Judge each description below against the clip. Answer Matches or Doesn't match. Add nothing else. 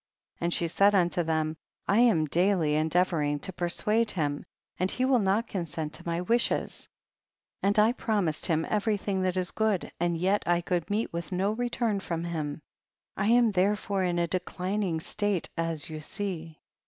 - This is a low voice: Doesn't match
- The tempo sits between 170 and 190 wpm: Matches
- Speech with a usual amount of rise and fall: Matches